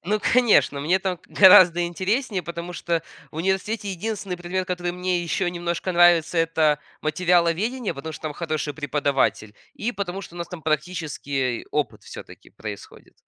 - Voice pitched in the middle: Yes, medium, 175 Hz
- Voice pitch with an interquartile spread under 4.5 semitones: Yes, average, 2.9 semitones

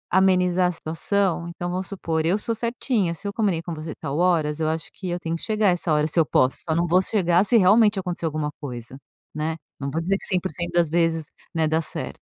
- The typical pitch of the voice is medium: Yes, medium, 170 Hz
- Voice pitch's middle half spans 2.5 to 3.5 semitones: Yes, average, 2.9 semitones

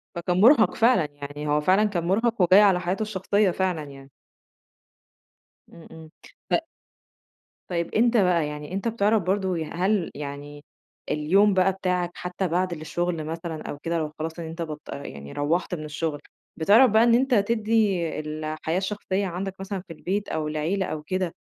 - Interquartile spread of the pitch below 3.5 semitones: No, average, 4.2 semitones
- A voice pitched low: No, medium, 180 Hz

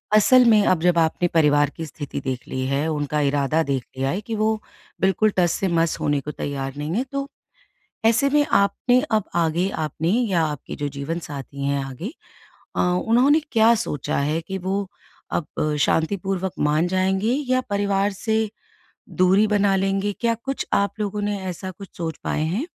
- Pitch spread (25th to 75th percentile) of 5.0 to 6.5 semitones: Yes, wide, 5.6 semitones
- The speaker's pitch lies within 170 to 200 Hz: Yes, medium, 185 Hz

